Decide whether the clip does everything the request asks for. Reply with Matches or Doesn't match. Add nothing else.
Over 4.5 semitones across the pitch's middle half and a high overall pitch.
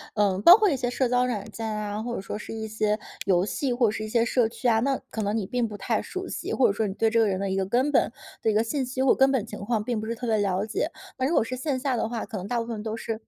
Doesn't match